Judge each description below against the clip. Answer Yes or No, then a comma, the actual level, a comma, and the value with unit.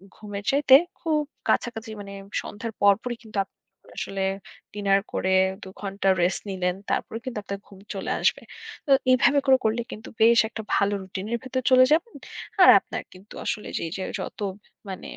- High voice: Yes, high, 210 Hz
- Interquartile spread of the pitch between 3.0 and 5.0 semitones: Yes, average, 3.7 semitones